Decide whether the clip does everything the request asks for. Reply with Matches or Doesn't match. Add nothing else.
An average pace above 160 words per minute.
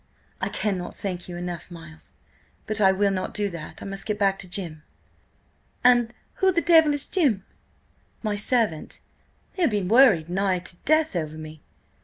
Matches